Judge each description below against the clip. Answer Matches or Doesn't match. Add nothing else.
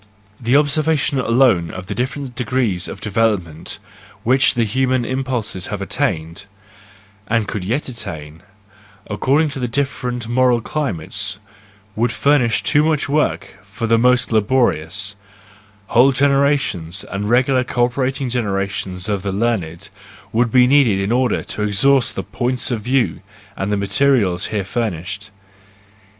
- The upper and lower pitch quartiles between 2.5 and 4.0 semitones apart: Doesn't match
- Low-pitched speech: Matches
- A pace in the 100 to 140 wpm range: Matches